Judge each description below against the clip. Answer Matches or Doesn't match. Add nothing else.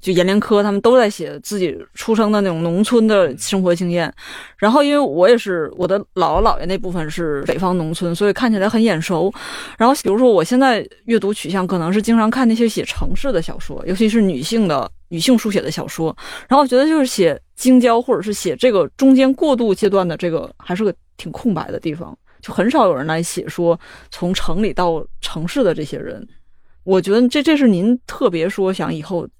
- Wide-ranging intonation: Doesn't match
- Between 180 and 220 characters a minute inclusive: Doesn't match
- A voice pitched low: Doesn't match